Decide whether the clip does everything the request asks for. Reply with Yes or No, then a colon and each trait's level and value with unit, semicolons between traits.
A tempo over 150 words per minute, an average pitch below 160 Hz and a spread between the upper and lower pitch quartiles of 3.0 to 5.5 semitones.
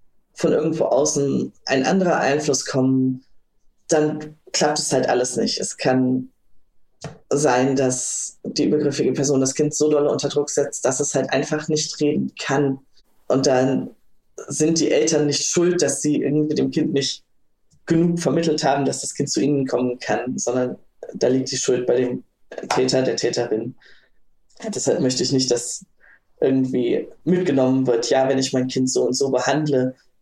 No: average, 165 wpm; medium, 140 Hz; narrow, 2.6 semitones